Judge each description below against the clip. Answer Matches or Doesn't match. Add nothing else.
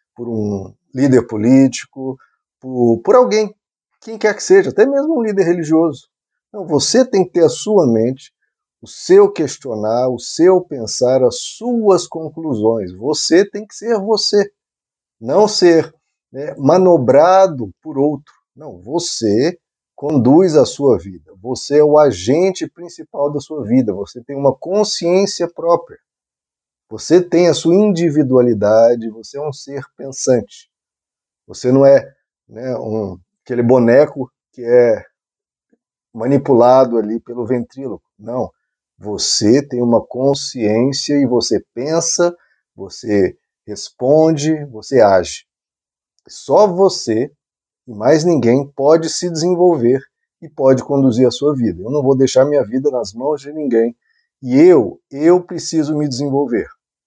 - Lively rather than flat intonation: Matches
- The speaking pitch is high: Doesn't match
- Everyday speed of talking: Matches